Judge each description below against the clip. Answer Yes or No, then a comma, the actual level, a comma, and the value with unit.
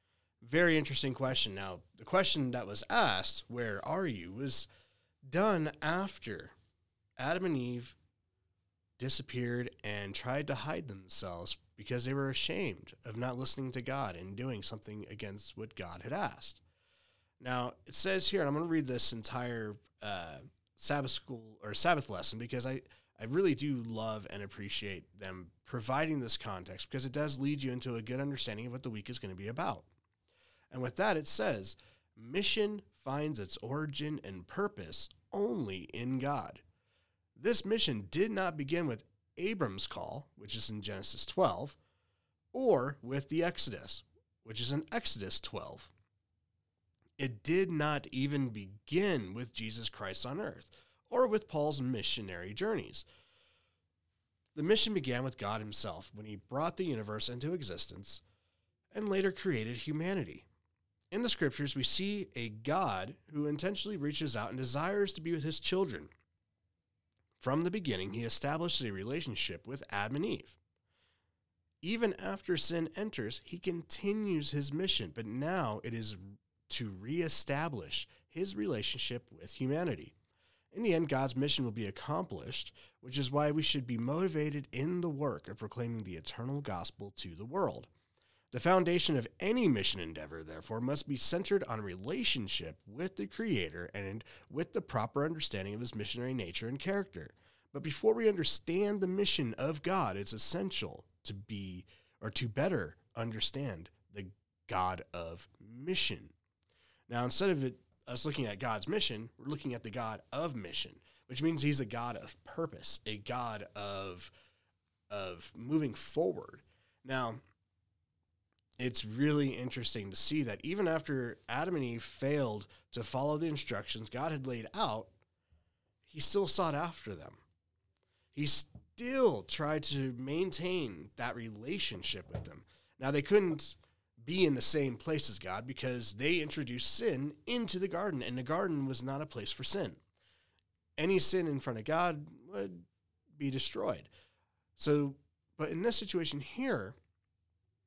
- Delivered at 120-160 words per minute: Yes, average, 155 wpm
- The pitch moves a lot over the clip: Yes, wide, 7.1 semitones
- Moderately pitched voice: No, low, 125 Hz